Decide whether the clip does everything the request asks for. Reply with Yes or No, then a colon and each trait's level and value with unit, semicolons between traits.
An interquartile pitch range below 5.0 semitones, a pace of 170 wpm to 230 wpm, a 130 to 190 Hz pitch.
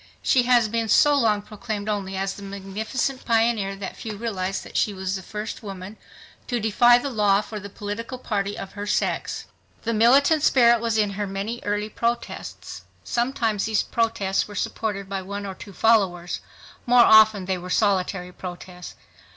No: average, 2.9 semitones; average, 175 wpm; high, 210 Hz